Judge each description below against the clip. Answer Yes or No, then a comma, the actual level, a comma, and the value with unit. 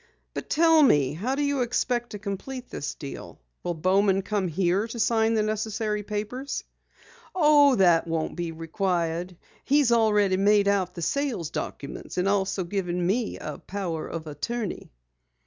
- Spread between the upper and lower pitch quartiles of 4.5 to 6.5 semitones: Yes, average, 5.1 semitones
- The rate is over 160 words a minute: No, average, 155 wpm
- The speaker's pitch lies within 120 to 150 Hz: No, high, 200 Hz